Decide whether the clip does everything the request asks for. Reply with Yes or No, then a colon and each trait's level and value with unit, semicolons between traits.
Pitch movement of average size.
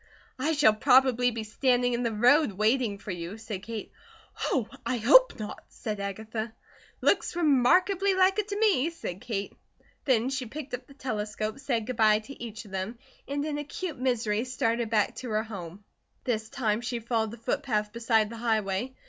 Yes: average, 3.9 semitones